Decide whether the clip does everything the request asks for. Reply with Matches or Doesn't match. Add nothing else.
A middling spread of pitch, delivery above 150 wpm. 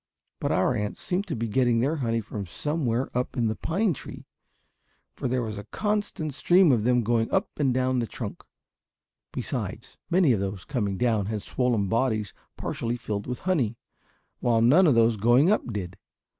Matches